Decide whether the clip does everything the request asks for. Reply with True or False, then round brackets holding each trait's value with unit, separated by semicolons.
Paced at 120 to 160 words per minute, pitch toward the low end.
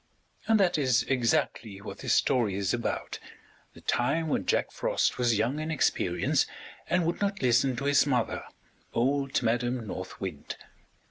True (155 wpm; 125 Hz)